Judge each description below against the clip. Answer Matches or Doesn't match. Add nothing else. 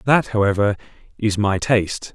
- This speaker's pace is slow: Matches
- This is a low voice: Matches